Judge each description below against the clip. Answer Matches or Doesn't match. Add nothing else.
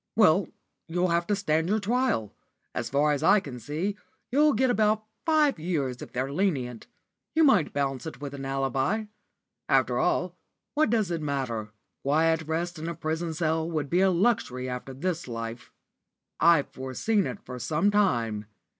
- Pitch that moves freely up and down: Matches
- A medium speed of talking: Matches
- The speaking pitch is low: Doesn't match